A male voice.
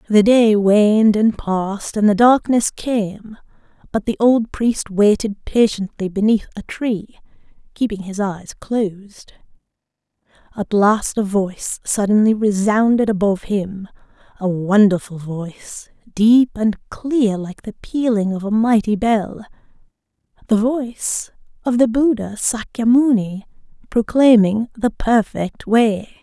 No: female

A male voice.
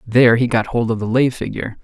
Yes: male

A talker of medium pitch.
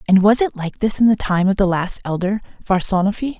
No: high, 200 Hz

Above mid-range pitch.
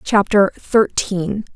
Yes: high, 200 Hz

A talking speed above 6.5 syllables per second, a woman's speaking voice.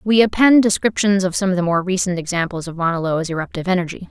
Yes: 6.7 syllables/s; female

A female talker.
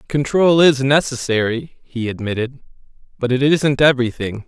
No: male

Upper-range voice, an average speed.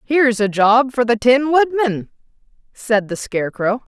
Yes: high, 240 Hz; average, 150 wpm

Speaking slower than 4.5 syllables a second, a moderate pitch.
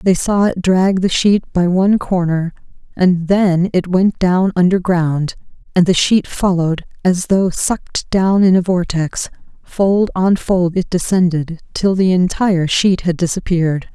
Yes: 4.2 syllables/s; medium, 180 Hz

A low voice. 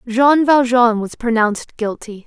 No: high, 235 Hz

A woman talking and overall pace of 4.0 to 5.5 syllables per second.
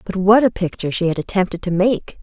No: female; 6.1 syllables/s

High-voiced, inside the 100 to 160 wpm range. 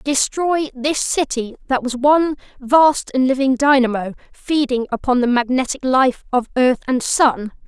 Yes: very high, 265 Hz; average, 150 wpm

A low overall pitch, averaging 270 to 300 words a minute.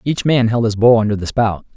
Yes: low, 115 Hz; fast, 275 wpm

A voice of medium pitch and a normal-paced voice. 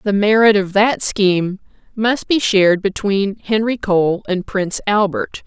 No: high, 205 Hz; average, 155 wpm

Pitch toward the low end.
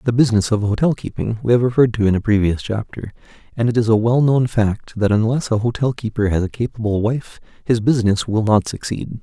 Yes: low, 115 Hz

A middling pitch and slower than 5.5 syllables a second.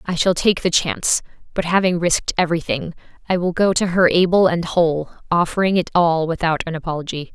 No: medium, 170 Hz; 5.9 syllables/s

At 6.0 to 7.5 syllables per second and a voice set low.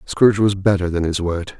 No: 5.4 syllables/s; very low, 95 Hz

